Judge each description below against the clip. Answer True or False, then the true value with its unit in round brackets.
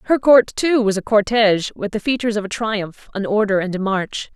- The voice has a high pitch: True (210 Hz)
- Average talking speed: False (235 wpm)